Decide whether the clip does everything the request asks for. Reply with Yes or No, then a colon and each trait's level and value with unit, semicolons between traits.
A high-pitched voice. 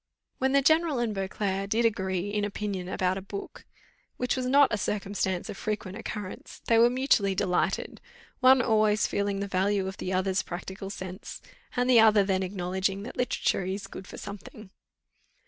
Yes: high, 200 Hz